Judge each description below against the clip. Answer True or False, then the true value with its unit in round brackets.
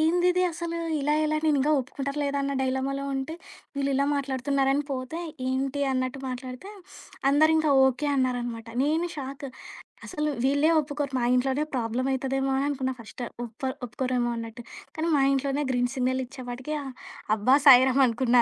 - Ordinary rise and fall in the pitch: False (2.0 semitones)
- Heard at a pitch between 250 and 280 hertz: True (270 Hz)